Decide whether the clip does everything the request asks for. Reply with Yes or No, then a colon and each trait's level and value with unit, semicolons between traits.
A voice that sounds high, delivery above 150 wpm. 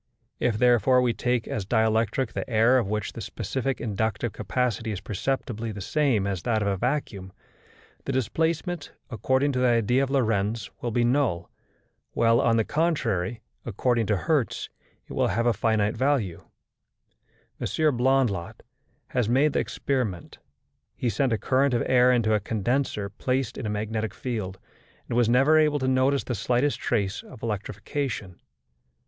No: low, 115 Hz; average, 160 wpm